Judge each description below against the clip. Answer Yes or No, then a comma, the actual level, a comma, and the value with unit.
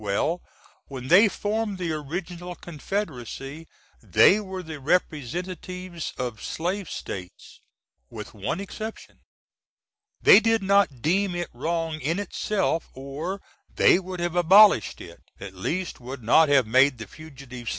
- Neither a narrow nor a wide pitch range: No, wide, 5.8 semitones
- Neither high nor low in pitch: Yes, medium, 165 Hz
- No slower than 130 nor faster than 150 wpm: Yes, slow, 135 wpm